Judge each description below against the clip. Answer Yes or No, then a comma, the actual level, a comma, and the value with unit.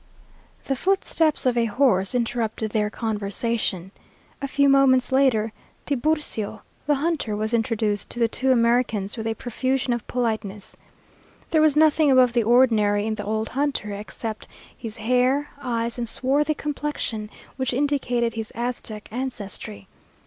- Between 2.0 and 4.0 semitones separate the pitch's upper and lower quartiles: Yes, average, 3.7 semitones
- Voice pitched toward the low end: No, high, 235 Hz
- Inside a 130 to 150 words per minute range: Yes, average, 140 wpm